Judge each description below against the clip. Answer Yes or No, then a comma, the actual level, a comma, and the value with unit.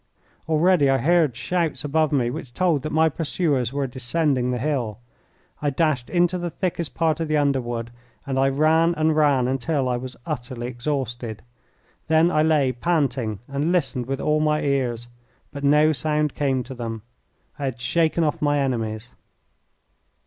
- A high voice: No, medium, 140 Hz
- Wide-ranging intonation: No, average, 3.9 semitones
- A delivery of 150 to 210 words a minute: Yes, average, 165 wpm